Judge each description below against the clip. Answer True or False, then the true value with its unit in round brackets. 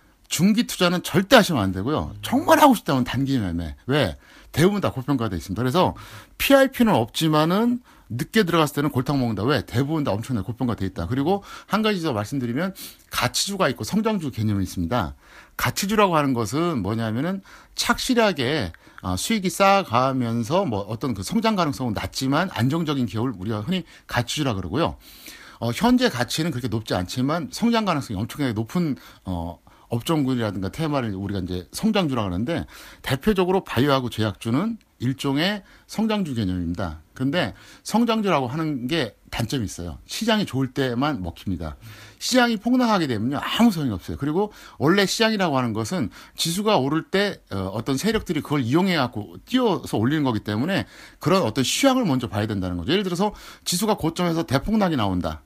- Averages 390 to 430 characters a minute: True (395 characters per minute)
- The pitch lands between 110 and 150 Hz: True (135 Hz)